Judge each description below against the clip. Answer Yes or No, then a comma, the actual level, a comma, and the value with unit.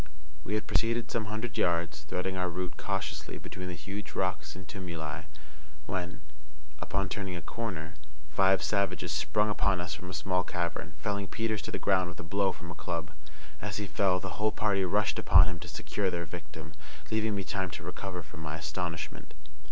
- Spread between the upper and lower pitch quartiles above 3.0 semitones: No, average, 2.7 semitones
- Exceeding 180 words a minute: Yes, average, 190 wpm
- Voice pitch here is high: No, very low, 90 Hz